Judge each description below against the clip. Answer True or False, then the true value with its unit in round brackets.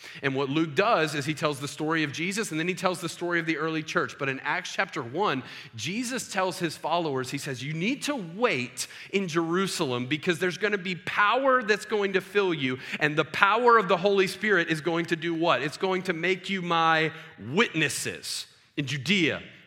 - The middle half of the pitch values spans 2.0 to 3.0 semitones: False (3.9 semitones)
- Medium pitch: True (170 Hz)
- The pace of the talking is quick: True (215 wpm)